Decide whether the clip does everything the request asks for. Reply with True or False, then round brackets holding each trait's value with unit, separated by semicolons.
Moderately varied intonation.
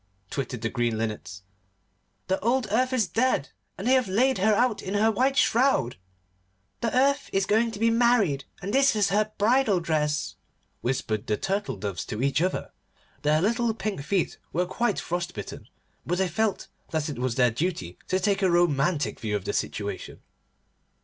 False (8.3 semitones)